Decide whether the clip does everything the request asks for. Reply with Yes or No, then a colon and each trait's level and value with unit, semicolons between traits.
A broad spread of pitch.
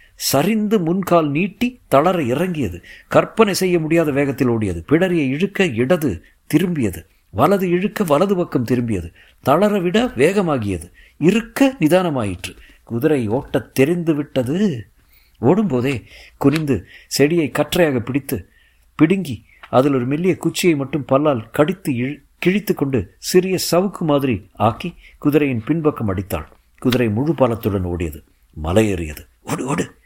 Yes: wide, 7.7 semitones